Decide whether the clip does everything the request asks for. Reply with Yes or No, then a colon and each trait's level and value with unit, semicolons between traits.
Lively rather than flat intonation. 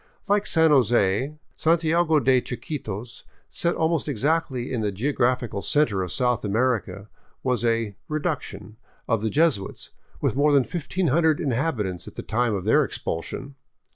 Yes: wide, 6.0 semitones